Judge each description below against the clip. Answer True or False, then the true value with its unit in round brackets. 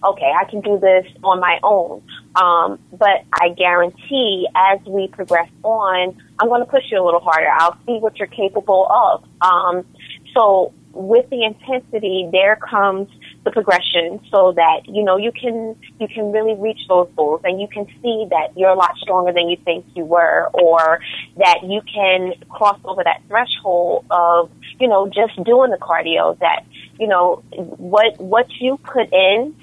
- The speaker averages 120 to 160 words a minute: False (180 wpm)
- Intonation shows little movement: False (3.6 semitones)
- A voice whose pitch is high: True (195 Hz)